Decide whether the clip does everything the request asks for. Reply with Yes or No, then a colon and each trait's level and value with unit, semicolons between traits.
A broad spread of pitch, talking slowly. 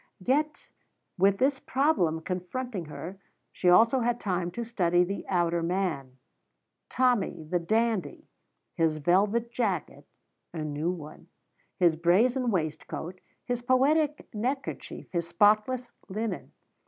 Yes: wide, 6.0 semitones; slow, 115 wpm